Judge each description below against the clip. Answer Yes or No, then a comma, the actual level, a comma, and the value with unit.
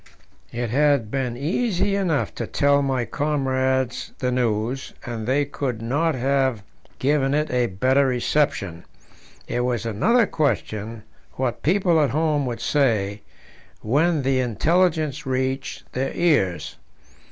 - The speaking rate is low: Yes, slow, 130 wpm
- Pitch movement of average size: Yes, average, 3.7 semitones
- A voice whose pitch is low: Yes, low, 130 Hz